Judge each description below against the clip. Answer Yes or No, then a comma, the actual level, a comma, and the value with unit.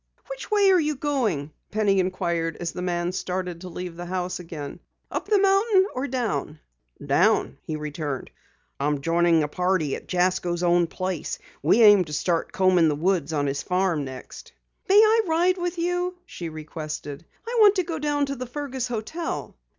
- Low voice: No, medium, 185 Hz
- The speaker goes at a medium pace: Yes, average, 180 wpm